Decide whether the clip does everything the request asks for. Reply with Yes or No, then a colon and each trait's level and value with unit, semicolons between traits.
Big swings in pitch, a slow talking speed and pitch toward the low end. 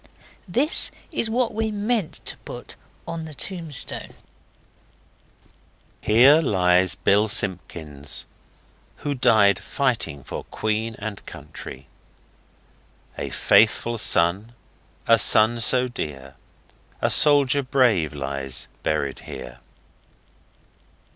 Yes: wide, 8.6 semitones; slow, 95 wpm; low, 110 Hz